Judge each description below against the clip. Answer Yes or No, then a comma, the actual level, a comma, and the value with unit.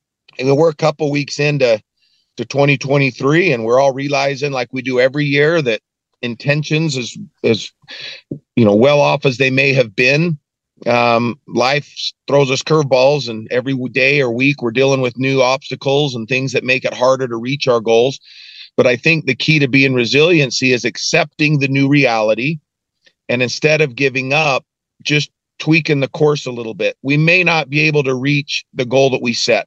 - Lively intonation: No, narrow, 2.5 semitones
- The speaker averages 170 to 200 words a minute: Yes, average, 190 wpm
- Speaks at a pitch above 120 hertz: Yes, low, 135 Hz